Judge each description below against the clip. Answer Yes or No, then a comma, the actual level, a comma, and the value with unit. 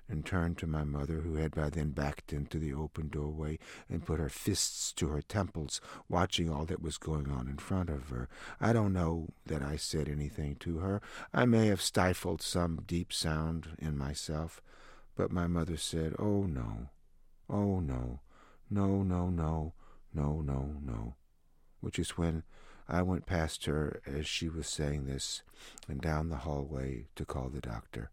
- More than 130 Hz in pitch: No, very low, 80 Hz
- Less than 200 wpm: Yes, average, 175 wpm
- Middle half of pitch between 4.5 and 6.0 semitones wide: No, average, 2.7 semitones